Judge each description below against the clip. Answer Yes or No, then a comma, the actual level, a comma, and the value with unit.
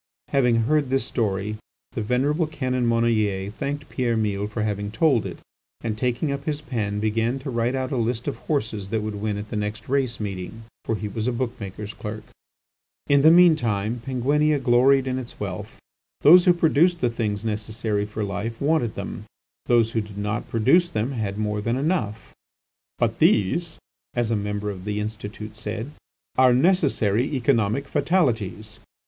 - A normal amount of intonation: Yes, average, 4.2 semitones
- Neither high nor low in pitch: No, low, 115 Hz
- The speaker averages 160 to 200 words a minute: Yes, average, 175 wpm